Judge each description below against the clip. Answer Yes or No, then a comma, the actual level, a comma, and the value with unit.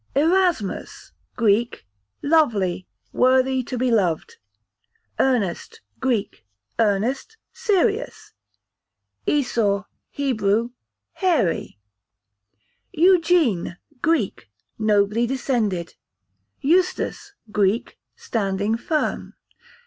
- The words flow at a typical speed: No, slow, 65 wpm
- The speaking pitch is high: Yes, high, 245 Hz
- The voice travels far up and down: Yes, wide, 7.8 semitones